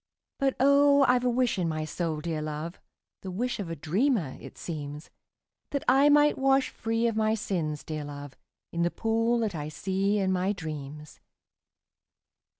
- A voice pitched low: No, high, 190 Hz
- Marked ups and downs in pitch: Yes, wide, 7.9 semitones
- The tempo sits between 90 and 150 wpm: No, average, 175 wpm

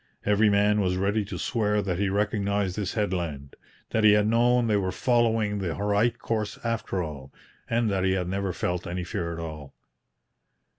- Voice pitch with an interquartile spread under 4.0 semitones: Yes, average, 2.8 semitones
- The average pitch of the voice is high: No, low, 100 Hz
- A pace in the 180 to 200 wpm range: Yes, average, 185 wpm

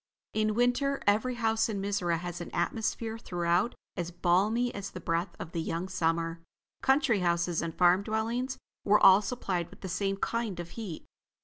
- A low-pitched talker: No, high, 195 Hz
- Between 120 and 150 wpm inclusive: No, average, 175 wpm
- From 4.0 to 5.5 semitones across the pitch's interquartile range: Yes, average, 4.4 semitones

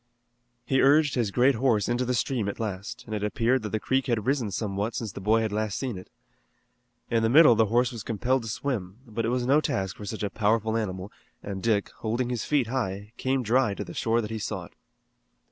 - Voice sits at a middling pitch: No, low, 115 Hz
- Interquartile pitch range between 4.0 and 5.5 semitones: No, average, 3.3 semitones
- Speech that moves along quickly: Yes, fast, 230 wpm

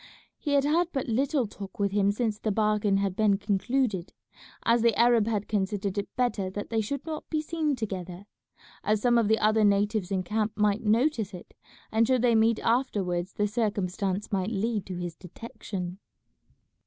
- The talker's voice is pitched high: Yes, high, 210 Hz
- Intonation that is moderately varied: Yes, average, 3.0 semitones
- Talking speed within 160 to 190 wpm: Yes, average, 180 wpm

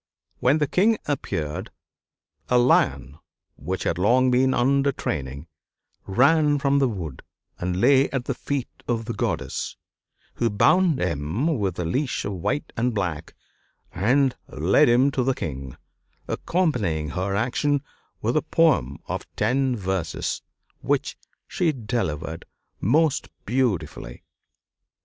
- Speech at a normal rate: No, slow, 130 wpm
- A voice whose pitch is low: Yes, low, 120 Hz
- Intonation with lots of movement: Yes, wide, 7.6 semitones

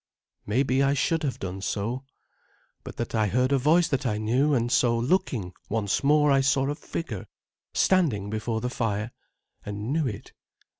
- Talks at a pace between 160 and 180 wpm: Yes, average, 170 wpm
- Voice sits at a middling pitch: No, low, 125 Hz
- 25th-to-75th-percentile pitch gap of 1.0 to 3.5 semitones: No, average, 4.6 semitones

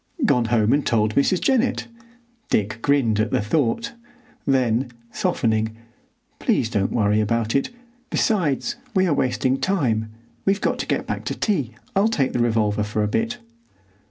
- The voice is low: Yes, low, 120 Hz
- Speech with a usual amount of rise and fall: No, wide, 6.7 semitones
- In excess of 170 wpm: No, average, 155 wpm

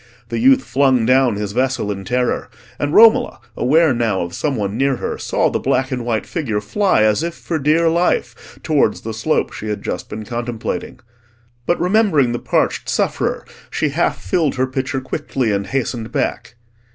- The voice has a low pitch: Yes, low, 130 Hz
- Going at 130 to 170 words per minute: No, average, 180 wpm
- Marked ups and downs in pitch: Yes, wide, 5.8 semitones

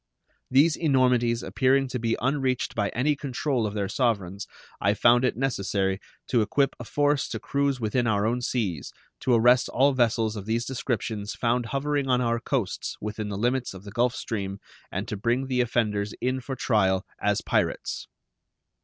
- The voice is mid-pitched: No, low, 120 Hz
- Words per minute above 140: Yes, average, 175 wpm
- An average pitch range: Yes, average, 3.7 semitones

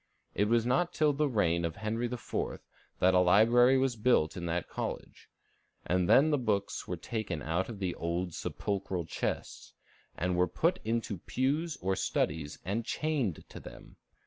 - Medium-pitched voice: No, low, 105 Hz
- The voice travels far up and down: Yes, wide, 5.9 semitones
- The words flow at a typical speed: Yes, average, 170 wpm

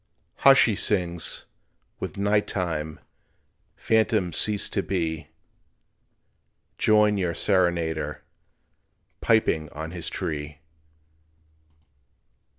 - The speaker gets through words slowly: Yes, slow, 80 wpm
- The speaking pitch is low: Yes, very low, 90 Hz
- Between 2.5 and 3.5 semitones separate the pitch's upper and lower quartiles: No, average, 4.6 semitones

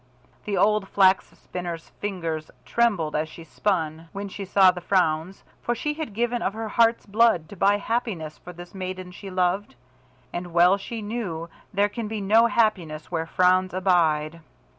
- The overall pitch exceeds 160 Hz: Yes, high, 190 Hz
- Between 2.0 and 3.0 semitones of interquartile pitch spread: No, average, 3.8 semitones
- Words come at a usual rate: Yes, average, 170 wpm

